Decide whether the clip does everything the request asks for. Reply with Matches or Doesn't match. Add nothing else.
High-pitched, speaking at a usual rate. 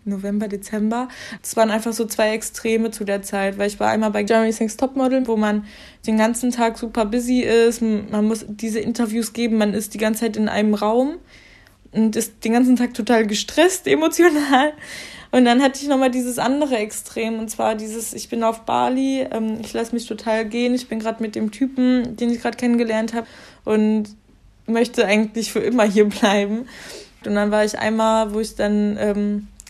Doesn't match